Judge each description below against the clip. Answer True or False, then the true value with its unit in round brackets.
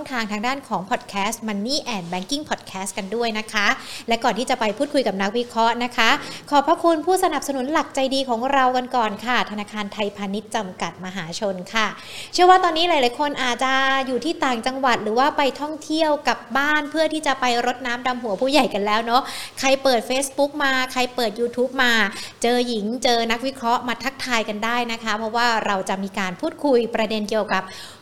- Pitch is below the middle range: False (245 Hz)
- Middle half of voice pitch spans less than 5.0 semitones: True (3.9 semitones)